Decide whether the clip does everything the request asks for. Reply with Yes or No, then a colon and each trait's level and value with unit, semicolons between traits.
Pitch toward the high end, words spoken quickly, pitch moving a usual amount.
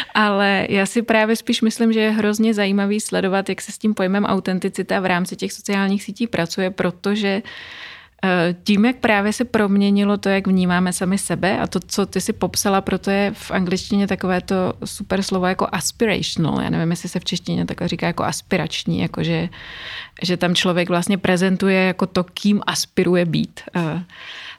No: high, 195 Hz; fast, 175 wpm; narrow, 2.2 semitones